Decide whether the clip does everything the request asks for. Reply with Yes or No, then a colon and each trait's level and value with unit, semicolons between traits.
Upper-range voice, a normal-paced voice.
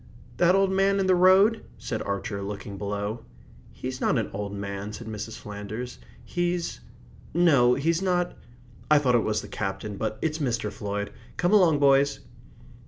No: low, 125 Hz; average, 165 wpm